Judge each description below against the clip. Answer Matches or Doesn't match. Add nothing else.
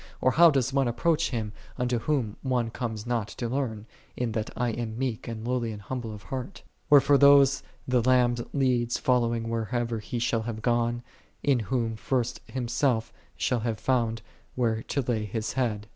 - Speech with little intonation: Matches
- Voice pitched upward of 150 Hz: Doesn't match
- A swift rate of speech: Doesn't match